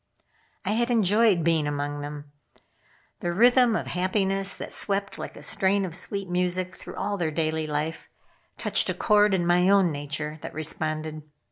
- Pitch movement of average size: Yes, average, 4.2 semitones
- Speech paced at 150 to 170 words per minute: Yes, average, 165 wpm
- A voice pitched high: No, medium, 180 Hz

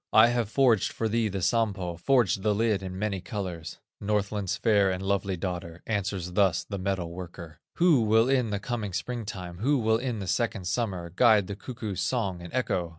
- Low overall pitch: Yes, low, 100 Hz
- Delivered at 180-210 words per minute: Yes, average, 195 wpm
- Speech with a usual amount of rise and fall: Yes, average, 3.6 semitones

